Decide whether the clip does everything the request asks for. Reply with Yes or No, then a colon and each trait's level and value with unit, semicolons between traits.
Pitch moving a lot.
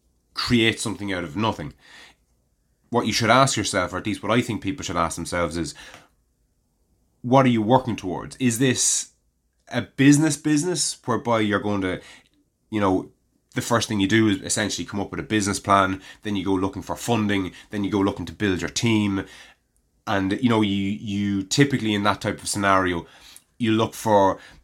No: average, 3.3 semitones